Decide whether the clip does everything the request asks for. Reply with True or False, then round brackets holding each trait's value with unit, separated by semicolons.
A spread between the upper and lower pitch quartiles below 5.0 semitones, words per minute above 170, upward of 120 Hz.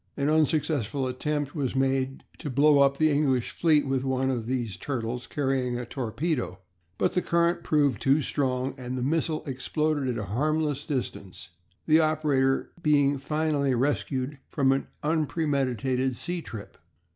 False (2.9 semitones; 150 wpm; 140 Hz)